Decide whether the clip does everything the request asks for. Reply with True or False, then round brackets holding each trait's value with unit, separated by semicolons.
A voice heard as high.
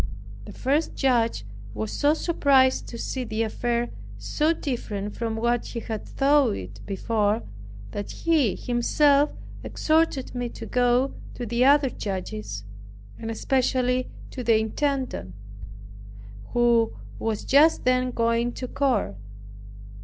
True (240 Hz)